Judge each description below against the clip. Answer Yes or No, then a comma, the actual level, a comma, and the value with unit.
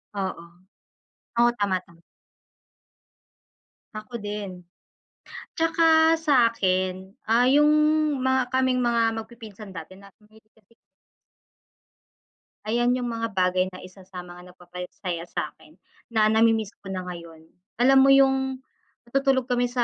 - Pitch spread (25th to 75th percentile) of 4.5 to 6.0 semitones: Yes, average, 5.2 semitones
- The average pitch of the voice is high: Yes, high, 220 Hz